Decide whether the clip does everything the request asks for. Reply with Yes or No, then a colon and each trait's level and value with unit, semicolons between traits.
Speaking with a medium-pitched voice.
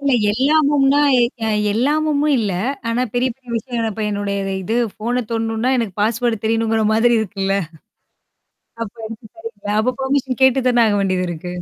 No: high, 230 Hz